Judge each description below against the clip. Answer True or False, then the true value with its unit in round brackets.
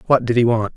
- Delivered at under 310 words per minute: False (315 wpm)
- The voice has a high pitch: False (120 Hz)